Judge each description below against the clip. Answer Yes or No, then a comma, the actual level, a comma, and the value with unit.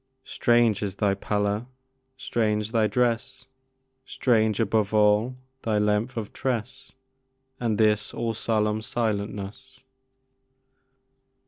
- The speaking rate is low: Yes, slow, 100 wpm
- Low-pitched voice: Yes, low, 110 Hz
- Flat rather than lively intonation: Yes, narrow, 2.0 semitones